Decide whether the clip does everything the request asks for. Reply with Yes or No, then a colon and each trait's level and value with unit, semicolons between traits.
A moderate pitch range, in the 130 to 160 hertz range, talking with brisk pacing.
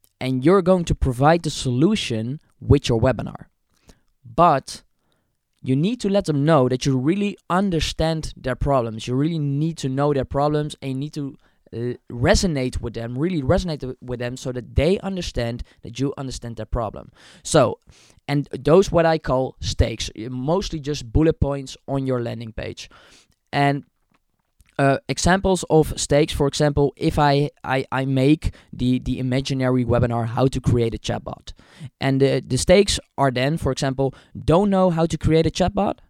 No: average, 3.9 semitones; low, 135 Hz; average, 170 wpm